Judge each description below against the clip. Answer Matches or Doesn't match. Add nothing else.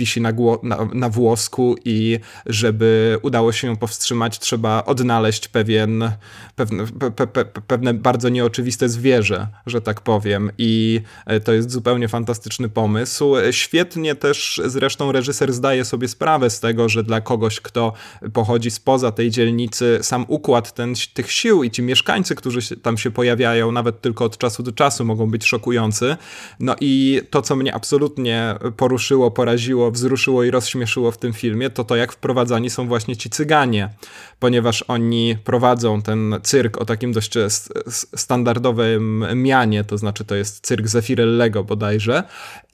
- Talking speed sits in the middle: Matches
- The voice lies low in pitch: Matches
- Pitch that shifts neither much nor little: Doesn't match